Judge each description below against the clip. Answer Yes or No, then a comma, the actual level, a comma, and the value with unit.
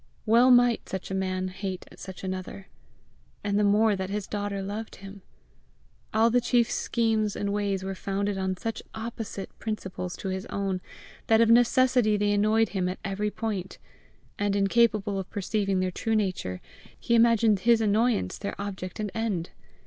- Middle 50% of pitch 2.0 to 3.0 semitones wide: Yes, narrow, 2.6 semitones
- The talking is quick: No, average, 165 wpm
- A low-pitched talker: No, high, 205 Hz